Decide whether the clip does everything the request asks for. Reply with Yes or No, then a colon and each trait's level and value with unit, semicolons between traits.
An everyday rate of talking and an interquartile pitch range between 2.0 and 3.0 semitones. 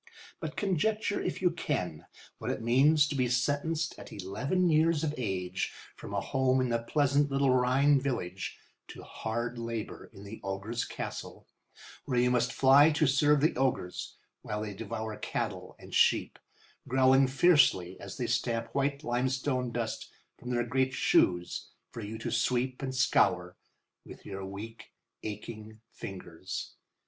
No: average, 155 wpm; average, 4.3 semitones